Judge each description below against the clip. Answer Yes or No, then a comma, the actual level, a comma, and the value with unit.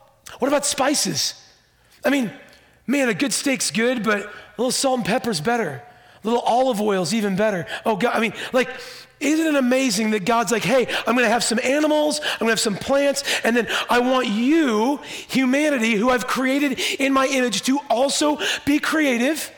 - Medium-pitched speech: No, very high, 255 Hz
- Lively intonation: No, average, 3.4 semitones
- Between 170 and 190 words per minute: Yes, average, 185 wpm